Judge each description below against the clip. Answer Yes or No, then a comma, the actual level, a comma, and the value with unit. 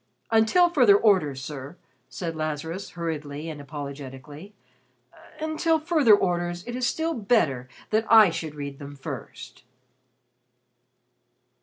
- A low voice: No, medium, 165 Hz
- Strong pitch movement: Yes, wide, 7.6 semitones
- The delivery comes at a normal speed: No, slow, 115 wpm